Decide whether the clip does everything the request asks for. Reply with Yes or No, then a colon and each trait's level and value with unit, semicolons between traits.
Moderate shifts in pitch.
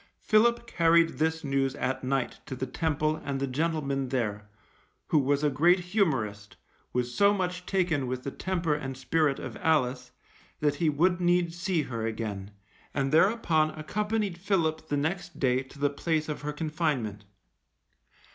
Yes: average, 4.5 semitones